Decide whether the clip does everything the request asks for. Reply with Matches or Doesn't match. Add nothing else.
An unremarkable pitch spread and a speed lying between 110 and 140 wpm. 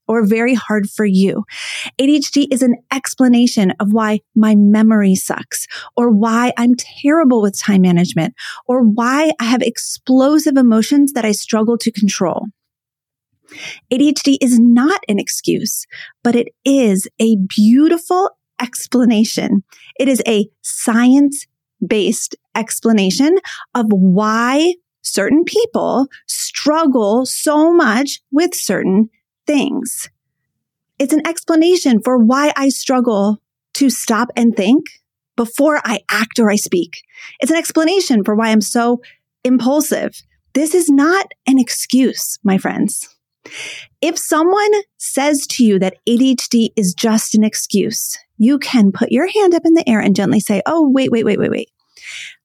Matches